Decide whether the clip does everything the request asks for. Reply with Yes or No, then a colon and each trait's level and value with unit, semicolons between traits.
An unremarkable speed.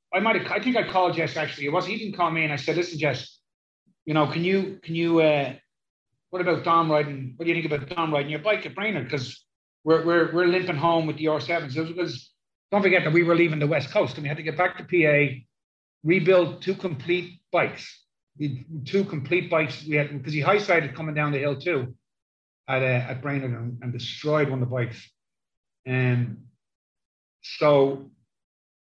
No: fast, 215 wpm